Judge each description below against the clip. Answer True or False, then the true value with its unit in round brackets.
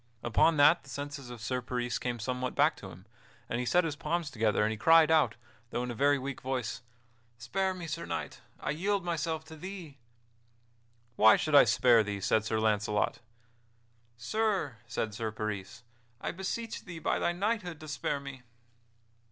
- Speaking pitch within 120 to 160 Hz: True (140 Hz)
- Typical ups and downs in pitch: False (6.2 semitones)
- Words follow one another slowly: False (180 wpm)